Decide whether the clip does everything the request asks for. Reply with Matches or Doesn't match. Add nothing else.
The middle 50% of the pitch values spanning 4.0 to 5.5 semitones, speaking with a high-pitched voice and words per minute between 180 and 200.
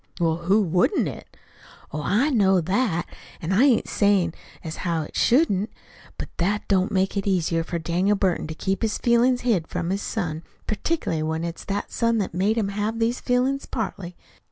Matches